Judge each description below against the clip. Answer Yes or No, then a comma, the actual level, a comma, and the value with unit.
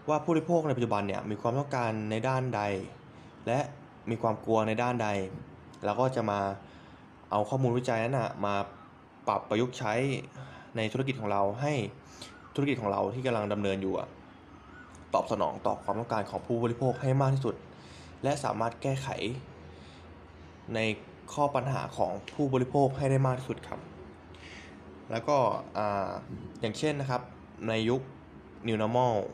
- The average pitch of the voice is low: Yes, low, 115 Hz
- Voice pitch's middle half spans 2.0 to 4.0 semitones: No, average, 4.7 semitones